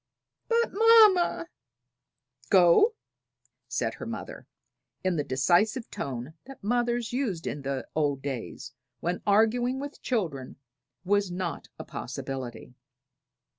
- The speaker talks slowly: Yes, slow, 115 wpm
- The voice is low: No, medium, 185 Hz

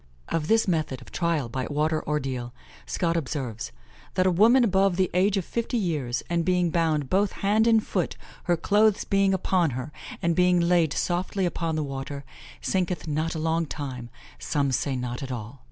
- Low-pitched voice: No, medium, 165 Hz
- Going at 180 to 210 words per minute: Yes, average, 185 wpm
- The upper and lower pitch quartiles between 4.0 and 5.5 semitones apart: Yes, average, 4.8 semitones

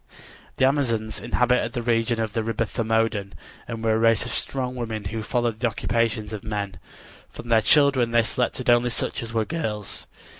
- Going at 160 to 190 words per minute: Yes, average, 185 wpm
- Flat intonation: Yes, narrow, 1.7 semitones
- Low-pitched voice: Yes, low, 115 Hz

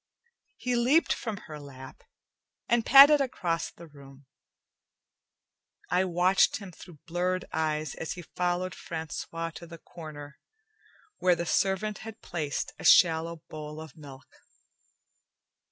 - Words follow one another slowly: Yes, slow, 125 wpm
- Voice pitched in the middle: Yes, medium, 170 Hz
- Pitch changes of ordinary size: Yes, average, 3.4 semitones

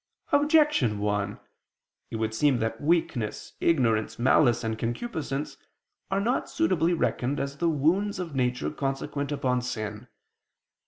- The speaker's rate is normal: No, slow, 125 wpm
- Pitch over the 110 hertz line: Yes, low, 135 Hz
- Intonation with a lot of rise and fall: Yes, wide, 6.5 semitones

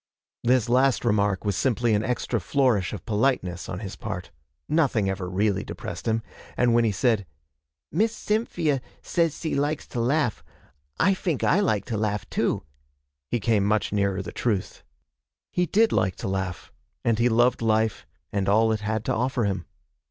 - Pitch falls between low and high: No, low, 110 Hz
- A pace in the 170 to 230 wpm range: Yes, average, 180 wpm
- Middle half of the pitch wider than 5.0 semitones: No, average, 4.3 semitones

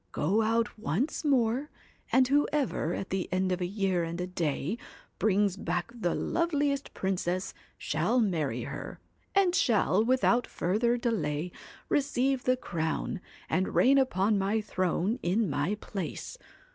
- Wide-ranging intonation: Yes, wide, 5.7 semitones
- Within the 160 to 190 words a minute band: No, average, 140 wpm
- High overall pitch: Yes, high, 205 Hz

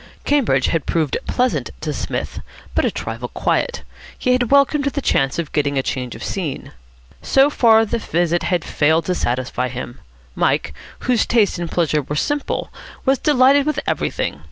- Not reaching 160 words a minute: No, average, 170 wpm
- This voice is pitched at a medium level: Yes, medium, 180 Hz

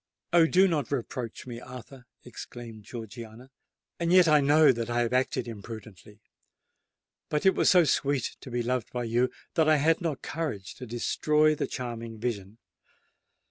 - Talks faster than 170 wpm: No, average, 165 wpm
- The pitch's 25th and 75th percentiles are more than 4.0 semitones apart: Yes, average, 4.7 semitones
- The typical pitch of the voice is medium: No, low, 125 Hz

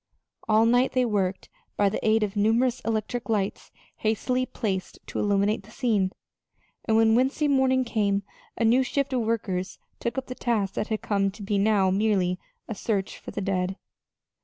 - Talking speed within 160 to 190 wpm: Yes, average, 180 wpm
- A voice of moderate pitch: No, high, 215 Hz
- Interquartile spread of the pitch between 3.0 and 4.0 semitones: Yes, average, 3.3 semitones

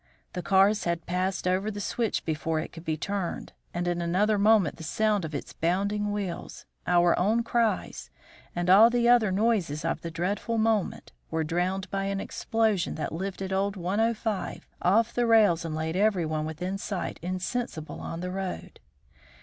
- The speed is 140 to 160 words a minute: No, average, 170 wpm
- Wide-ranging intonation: No, average, 3.6 semitones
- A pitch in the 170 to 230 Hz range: Yes, high, 190 Hz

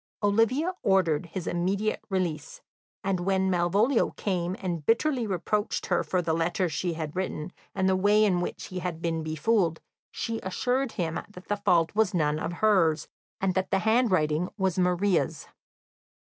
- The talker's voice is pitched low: No, medium, 185 Hz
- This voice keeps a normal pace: Yes, average, 160 wpm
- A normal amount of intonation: Yes, average, 3.4 semitones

